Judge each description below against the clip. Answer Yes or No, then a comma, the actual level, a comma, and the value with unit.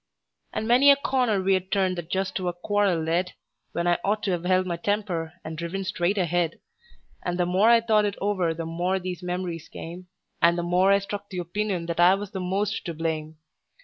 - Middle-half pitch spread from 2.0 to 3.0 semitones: Yes, average, 2.7 semitones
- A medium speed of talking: No, fast, 215 wpm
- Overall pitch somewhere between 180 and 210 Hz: Yes, medium, 185 Hz